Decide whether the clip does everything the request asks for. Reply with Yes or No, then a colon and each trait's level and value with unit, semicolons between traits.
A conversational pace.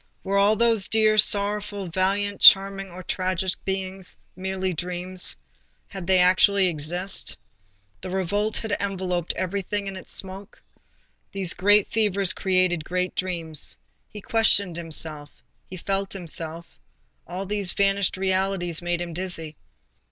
No: slow, 130 wpm